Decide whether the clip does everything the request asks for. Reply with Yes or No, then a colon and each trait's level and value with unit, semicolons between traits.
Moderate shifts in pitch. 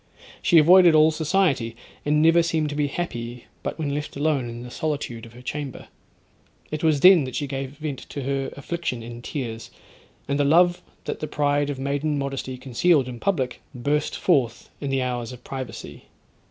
Yes: average, 3.5 semitones